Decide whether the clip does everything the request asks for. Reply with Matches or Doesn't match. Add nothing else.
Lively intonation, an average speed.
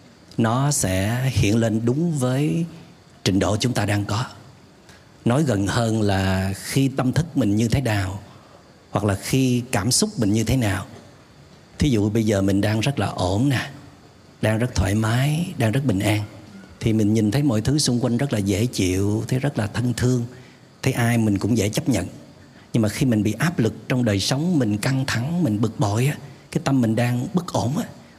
Doesn't match